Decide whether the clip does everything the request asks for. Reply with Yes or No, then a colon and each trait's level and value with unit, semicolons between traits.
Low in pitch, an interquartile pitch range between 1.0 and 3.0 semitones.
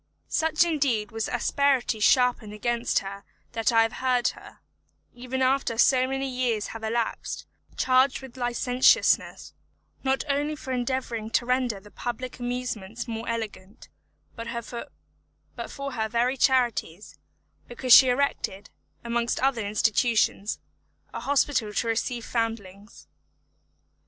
No: high, 240 Hz; narrow, 2.5 semitones